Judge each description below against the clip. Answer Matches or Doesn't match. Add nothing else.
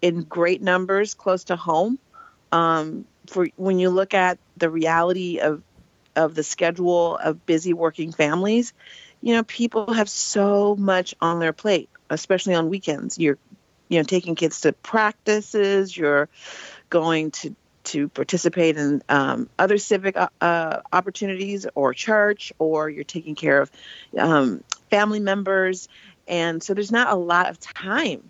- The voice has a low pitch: Doesn't match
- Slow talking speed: Doesn't match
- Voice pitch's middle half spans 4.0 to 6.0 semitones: Doesn't match